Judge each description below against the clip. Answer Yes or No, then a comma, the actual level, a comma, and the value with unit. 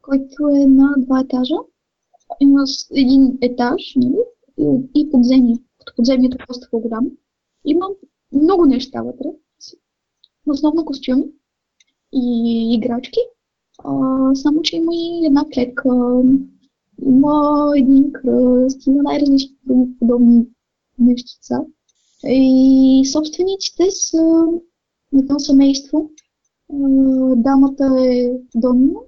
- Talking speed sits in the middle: No, slow, 95 wpm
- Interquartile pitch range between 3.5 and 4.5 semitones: No, average, 2.8 semitones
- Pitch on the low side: No, very high, 270 Hz